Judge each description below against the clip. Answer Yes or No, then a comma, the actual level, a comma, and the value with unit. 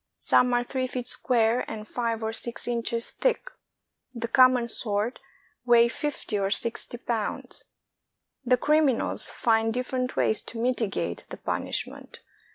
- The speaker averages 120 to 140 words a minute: Yes, slow, 135 wpm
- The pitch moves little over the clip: Yes, narrow, 2.0 semitones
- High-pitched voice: Yes, high, 240 Hz